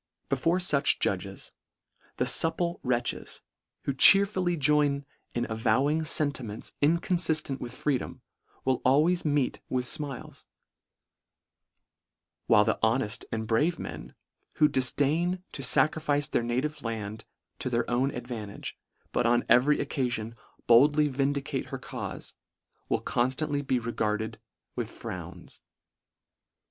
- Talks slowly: Yes, slow, 115 wpm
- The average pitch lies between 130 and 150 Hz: Yes, low, 135 Hz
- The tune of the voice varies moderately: Yes, average, 4.2 semitones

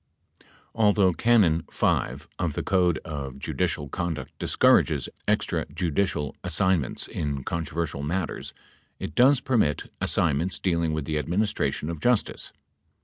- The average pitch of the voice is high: No, very low, 85 Hz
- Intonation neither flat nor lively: Yes, average, 4.2 semitones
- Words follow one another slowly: Yes, slow, 130 wpm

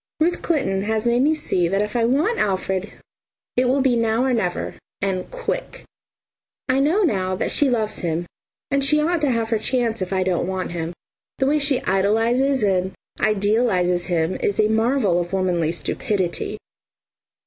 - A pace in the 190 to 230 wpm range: No, average, 175 wpm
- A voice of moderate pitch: No, high, 215 Hz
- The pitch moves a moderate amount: No, wide, 6.1 semitones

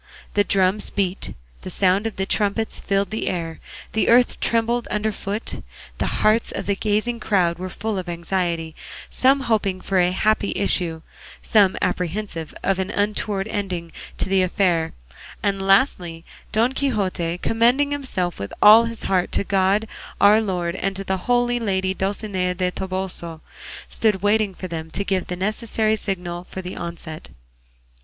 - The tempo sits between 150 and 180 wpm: Yes, average, 160 wpm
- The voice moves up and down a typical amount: Yes, average, 3.0 semitones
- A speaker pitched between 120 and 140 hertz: No, high, 195 Hz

